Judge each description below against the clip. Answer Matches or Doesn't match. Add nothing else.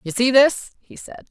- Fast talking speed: Matches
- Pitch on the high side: Matches